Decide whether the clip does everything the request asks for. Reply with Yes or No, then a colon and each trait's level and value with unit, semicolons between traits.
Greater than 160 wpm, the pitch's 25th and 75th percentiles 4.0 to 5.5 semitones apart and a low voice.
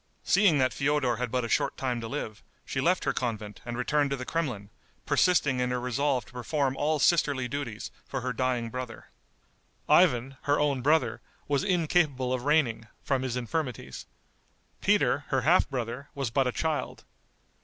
No: average, 175 wpm; average, 3.0 semitones; low, 130 Hz